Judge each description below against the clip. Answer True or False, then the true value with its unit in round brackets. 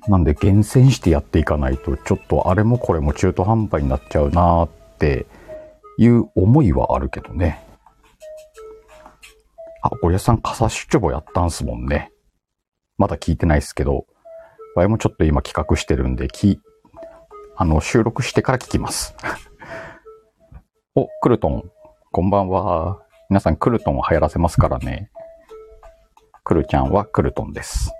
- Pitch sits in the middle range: False (100 Hz)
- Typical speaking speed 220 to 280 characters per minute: False (310 characters per minute)